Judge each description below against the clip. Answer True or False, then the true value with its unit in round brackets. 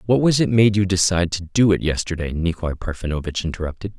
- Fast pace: False (195 wpm)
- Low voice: True (90 Hz)